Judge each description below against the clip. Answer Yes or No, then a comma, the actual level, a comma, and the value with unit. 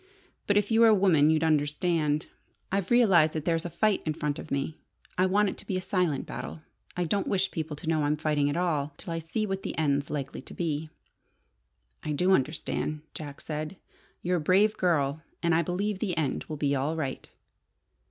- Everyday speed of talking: No, fast, 210 wpm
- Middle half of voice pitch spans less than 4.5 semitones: Yes, average, 3.7 semitones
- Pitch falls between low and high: Yes, medium, 160 Hz